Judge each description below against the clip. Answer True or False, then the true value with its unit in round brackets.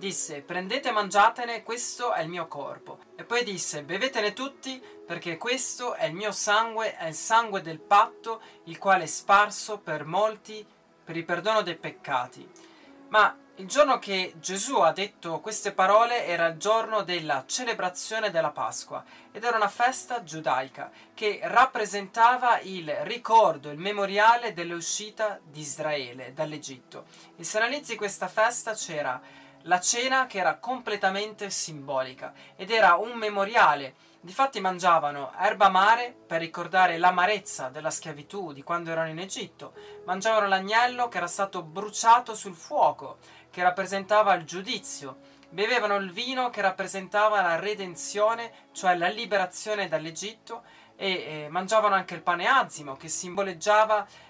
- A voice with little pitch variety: False (4.7 semitones)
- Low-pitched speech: False (195 Hz)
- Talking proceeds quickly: False (145 wpm)